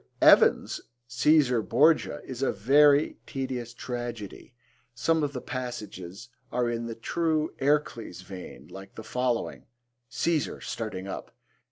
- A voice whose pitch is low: Yes, low, 125 Hz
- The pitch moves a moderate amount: Yes, average, 4.0 semitones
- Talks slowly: Yes, slow, 130 wpm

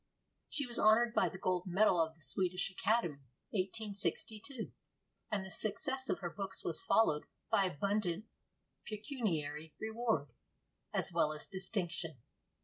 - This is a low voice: No, high, 195 Hz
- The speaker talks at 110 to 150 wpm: Yes, slow, 135 wpm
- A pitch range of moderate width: Yes, average, 4.6 semitones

